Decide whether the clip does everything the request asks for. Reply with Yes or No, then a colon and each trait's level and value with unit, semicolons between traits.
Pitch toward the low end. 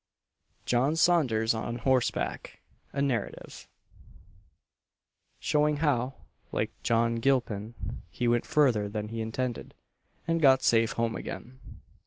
Yes: low, 120 Hz